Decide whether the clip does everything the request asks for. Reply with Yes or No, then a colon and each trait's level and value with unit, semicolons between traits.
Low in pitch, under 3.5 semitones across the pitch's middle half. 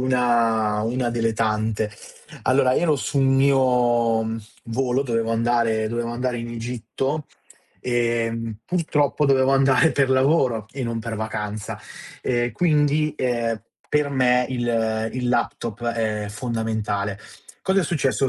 Yes: low, 120 Hz; average, 2.9 semitones